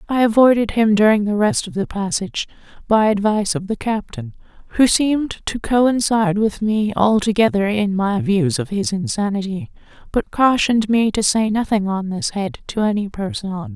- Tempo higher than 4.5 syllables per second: Yes, 5.1 syllables/s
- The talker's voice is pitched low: No, high, 210 Hz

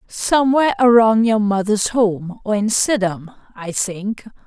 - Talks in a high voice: Yes, high, 215 Hz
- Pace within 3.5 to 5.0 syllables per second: Yes, 4.1 syllables/s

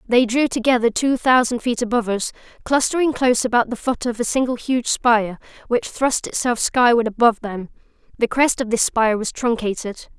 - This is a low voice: No, high, 240 Hz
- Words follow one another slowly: No, average, 185 wpm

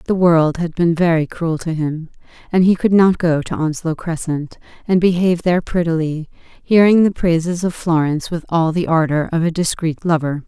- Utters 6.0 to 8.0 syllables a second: No, 5.1 syllables/s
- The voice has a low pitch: No, medium, 165 Hz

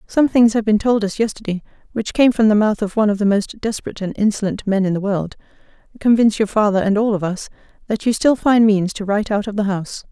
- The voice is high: Yes, high, 210 Hz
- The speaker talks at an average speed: No, fast, 250 wpm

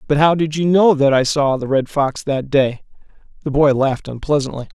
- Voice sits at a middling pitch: Yes, medium, 145 Hz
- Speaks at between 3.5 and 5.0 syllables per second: No, 5.3 syllables/s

